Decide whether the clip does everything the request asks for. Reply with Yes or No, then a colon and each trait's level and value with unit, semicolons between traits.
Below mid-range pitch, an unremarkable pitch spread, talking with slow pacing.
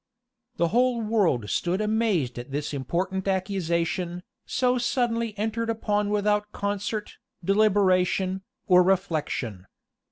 No: high, 195 Hz; average, 3.7 semitones; slow, 105 wpm